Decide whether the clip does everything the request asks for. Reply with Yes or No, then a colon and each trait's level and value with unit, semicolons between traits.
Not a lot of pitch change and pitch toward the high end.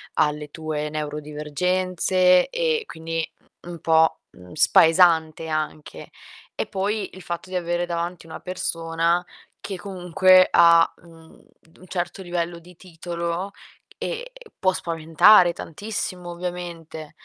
No: narrow, 2.1 semitones; medium, 170 Hz